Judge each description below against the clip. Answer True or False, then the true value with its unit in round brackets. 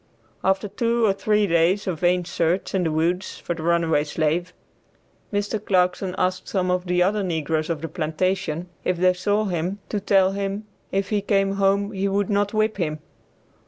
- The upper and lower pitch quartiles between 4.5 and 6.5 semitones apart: False (2.8 semitones)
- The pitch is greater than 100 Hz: True (185 Hz)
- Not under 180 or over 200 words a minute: True (185 wpm)